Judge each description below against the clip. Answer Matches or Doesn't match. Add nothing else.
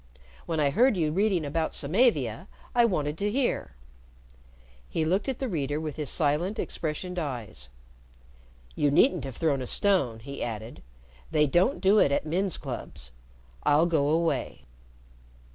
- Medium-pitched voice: Matches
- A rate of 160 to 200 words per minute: Doesn't match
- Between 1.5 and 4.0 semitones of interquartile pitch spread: Doesn't match